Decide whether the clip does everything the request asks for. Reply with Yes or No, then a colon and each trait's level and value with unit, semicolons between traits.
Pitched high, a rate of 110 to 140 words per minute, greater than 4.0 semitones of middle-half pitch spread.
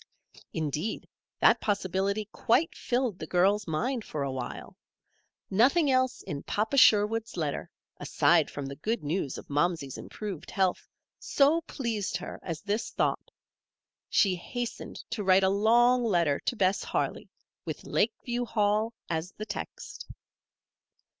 Yes: high, 205 Hz; slow, 135 wpm; average, 5.2 semitones